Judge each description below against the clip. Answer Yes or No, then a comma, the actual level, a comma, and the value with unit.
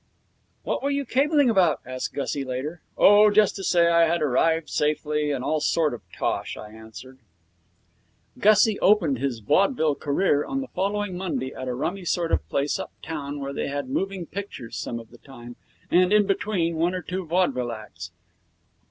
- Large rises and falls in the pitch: Yes, wide, 6.1 semitones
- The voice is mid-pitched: Yes, medium, 165 Hz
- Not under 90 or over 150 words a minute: No, average, 180 wpm